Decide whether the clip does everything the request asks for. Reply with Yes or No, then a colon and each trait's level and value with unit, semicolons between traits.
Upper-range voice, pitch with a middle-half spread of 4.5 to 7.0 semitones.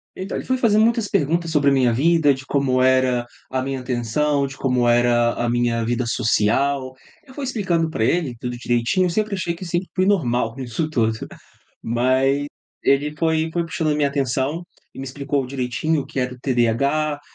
No: medium, 140 Hz; average, 4.8 semitones